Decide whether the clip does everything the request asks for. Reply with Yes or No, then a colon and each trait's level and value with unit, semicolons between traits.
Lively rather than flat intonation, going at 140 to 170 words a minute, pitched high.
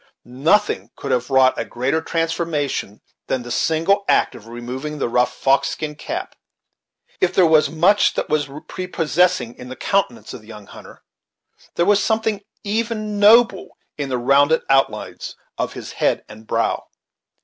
No: wide, 7.5 semitones; average, 160 wpm; medium, 155 Hz